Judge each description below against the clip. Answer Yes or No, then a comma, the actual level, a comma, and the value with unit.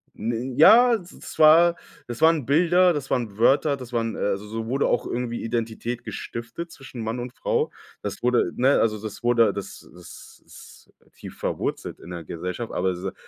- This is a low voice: Yes, low, 120 Hz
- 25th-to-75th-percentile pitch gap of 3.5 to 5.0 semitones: Yes, average, 4.3 semitones